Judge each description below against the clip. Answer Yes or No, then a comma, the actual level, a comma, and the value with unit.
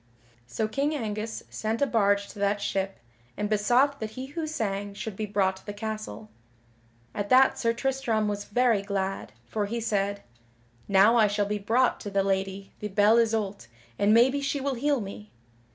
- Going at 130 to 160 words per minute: No, average, 185 wpm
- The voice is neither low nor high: No, high, 215 Hz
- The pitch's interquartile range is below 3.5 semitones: Yes, average, 2.8 semitones